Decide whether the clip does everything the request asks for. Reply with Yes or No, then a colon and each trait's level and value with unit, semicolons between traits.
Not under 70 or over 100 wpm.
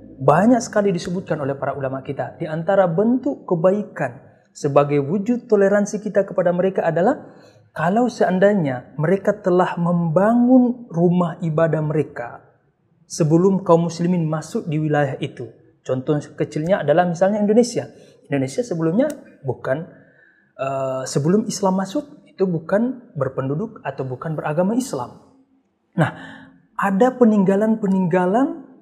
No: average, 115 wpm